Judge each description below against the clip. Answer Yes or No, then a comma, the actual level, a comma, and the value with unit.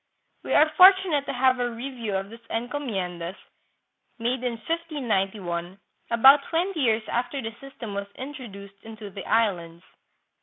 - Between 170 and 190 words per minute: No, average, 145 wpm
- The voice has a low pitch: No, high, 235 Hz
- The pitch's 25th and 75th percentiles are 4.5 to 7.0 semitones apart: Yes, wide, 5.5 semitones